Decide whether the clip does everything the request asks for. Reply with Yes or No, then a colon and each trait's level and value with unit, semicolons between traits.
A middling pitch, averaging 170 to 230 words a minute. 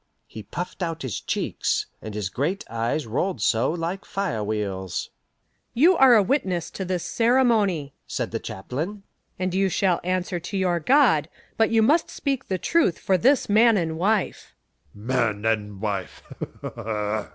No: medium, 175 Hz; average, 155 wpm